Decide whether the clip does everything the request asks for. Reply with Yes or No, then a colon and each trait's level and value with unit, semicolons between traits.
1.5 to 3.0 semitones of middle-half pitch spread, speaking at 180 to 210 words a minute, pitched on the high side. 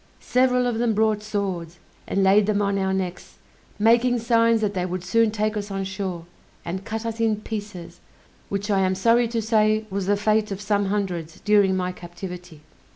Yes: average, 2.7 semitones; average, 190 wpm; high, 205 Hz